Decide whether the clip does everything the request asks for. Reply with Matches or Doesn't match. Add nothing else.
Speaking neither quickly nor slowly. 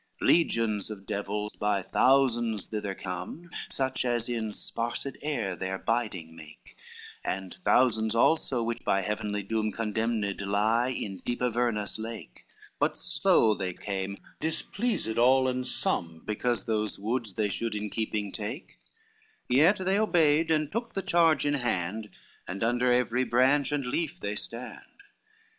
Matches